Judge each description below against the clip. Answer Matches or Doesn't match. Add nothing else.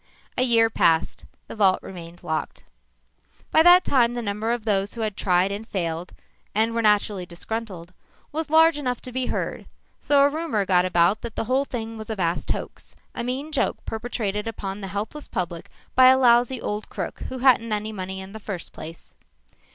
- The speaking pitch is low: Doesn't match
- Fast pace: Doesn't match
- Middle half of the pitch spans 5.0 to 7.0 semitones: Doesn't match